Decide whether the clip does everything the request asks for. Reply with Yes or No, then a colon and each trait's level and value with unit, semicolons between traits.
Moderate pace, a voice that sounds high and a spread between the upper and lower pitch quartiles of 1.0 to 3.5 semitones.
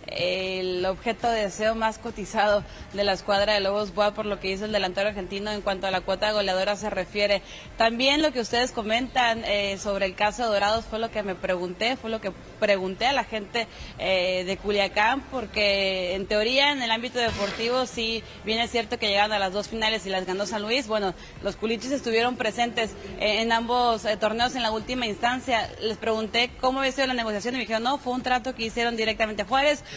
No: fast, 215 wpm; high, 215 Hz; average, 2.7 semitones